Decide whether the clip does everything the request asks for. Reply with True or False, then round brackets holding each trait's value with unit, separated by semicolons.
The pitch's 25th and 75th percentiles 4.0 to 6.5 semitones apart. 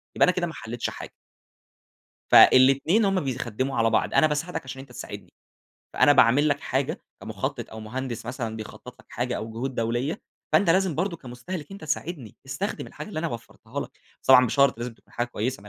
True (4.8 semitones)